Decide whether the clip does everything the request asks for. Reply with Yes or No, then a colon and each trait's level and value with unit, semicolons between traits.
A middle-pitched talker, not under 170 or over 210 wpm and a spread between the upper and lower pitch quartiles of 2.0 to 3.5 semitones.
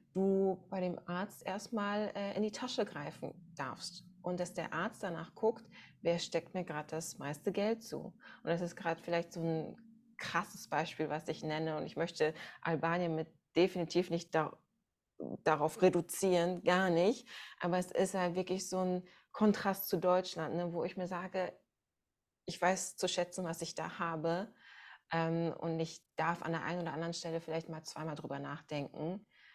Yes: medium, 175 Hz; average, 175 wpm; narrow, 2.5 semitones